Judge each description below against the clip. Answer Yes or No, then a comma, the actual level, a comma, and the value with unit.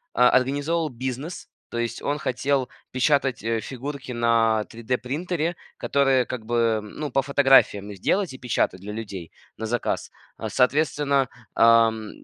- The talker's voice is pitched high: No, low, 125 Hz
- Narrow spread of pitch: No, average, 3.7 semitones